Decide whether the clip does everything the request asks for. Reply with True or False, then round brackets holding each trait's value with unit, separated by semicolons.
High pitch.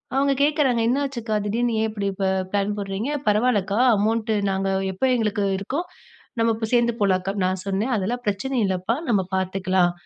True (210 Hz)